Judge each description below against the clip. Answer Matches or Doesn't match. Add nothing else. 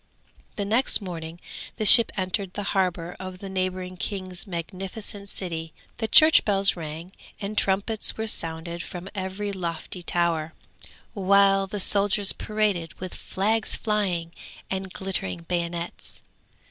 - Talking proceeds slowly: Matches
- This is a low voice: Doesn't match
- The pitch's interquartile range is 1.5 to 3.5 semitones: Matches